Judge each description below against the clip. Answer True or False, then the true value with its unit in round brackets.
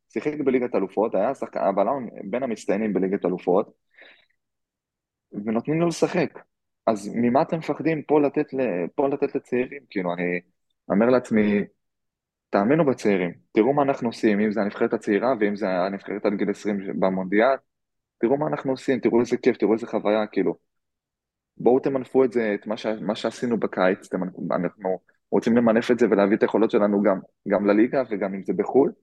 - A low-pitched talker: True (115 Hz)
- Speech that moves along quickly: True (165 wpm)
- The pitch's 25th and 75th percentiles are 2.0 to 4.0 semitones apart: False (4.6 semitones)